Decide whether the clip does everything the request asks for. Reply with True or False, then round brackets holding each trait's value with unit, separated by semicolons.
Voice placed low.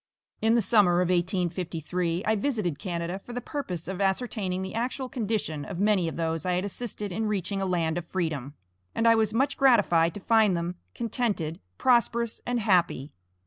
False (190 Hz)